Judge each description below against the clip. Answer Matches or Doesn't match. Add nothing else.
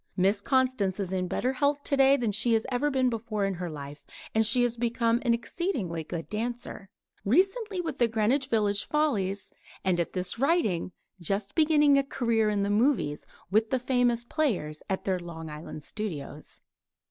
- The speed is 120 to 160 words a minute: Doesn't match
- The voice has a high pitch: Matches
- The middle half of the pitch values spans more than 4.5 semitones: Matches